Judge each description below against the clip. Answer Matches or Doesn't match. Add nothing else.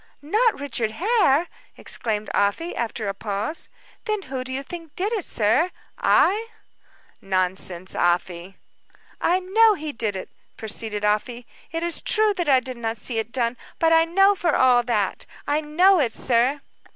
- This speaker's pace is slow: Doesn't match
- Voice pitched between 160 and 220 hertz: Doesn't match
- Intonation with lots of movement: Matches